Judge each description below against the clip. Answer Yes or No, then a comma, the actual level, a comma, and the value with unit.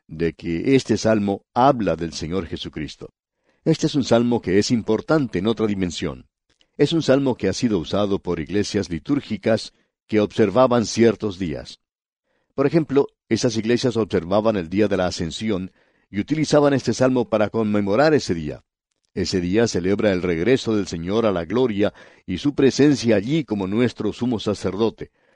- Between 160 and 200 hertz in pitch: No, low, 110 Hz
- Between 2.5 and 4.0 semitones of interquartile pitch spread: No, average, 4.6 semitones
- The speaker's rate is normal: Yes, average, 160 wpm